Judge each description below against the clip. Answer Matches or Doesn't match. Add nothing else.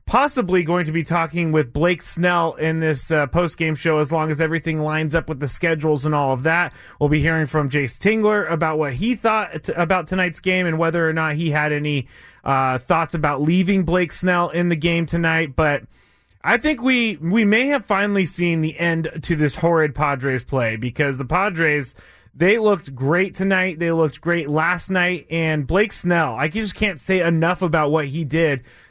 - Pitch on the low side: Doesn't match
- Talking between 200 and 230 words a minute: Matches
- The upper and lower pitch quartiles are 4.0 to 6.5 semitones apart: Doesn't match